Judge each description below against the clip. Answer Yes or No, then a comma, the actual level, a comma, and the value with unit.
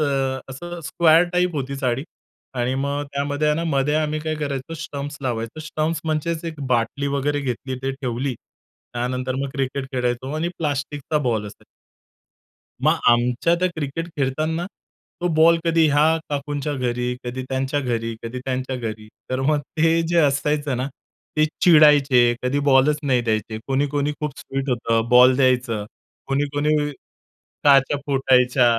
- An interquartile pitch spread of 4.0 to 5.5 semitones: No, average, 3.0 semitones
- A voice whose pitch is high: No, medium, 140 Hz